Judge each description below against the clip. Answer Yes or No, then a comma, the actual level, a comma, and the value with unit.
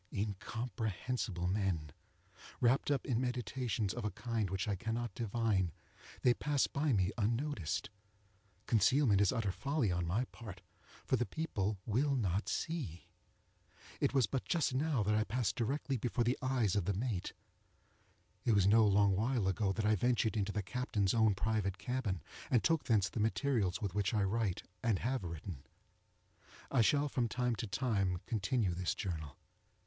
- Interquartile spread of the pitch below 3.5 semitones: No, average, 4.3 semitones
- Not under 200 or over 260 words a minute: No, average, 165 wpm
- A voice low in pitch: Yes, low, 110 Hz